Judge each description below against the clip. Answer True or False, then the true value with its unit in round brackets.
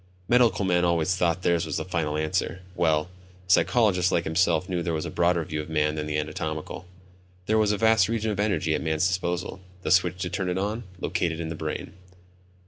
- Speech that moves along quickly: True (210 wpm)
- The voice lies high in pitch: False (90 Hz)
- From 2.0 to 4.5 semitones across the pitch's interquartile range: True (2.9 semitones)